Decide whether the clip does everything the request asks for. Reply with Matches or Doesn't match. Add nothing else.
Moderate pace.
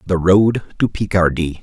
Matches